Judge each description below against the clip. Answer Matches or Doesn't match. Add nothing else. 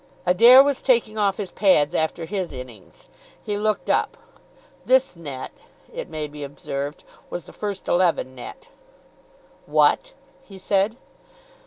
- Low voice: Doesn't match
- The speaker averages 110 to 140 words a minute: Matches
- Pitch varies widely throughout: Matches